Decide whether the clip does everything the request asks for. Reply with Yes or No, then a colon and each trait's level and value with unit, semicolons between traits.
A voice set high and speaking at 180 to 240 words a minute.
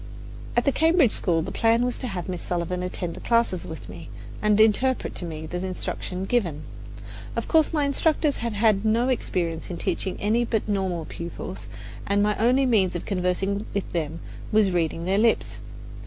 Yes: high, 200 Hz; average, 185 wpm